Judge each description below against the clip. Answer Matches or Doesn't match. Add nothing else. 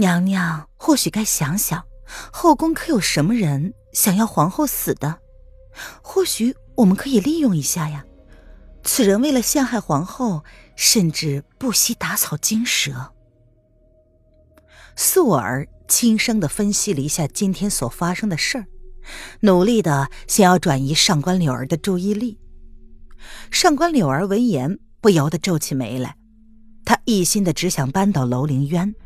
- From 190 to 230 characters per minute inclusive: Matches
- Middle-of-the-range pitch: Matches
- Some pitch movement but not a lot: Doesn't match